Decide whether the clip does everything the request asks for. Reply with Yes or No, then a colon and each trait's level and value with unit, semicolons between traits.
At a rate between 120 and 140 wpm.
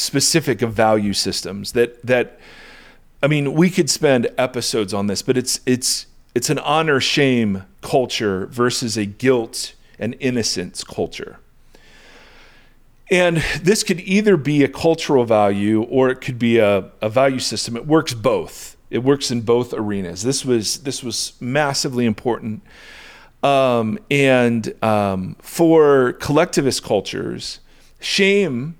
Yes: slow, 135 wpm